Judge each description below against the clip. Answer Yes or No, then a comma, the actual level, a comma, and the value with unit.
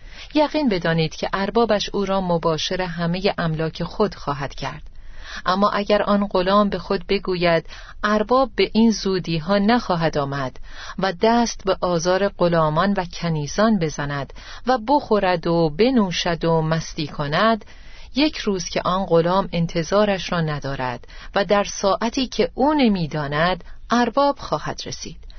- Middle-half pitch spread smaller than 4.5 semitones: Yes, average, 4.0 semitones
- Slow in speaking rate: No, average, 135 wpm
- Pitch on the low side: No, high, 190 Hz